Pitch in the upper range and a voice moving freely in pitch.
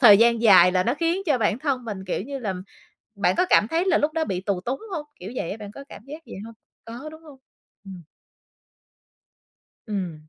Yes: high, 230 Hz; wide, 7.0 semitones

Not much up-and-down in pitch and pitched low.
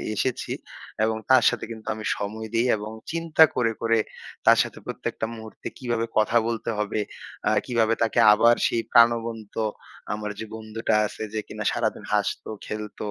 Yes: narrow, 1.4 semitones; low, 115 Hz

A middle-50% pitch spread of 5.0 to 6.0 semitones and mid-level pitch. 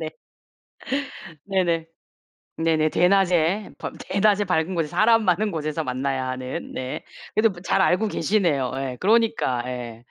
No: wide, 6.7 semitones; medium, 165 Hz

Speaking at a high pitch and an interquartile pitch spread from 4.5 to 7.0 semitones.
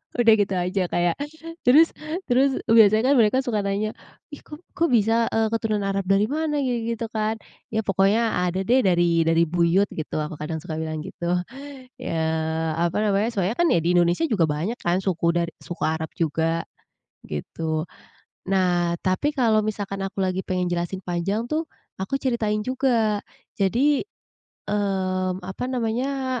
Yes: high, 195 Hz; average, 4.9 semitones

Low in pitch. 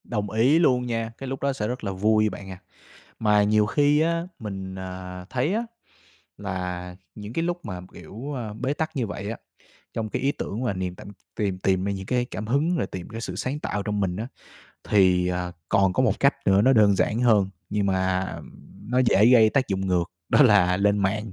Yes: low, 105 Hz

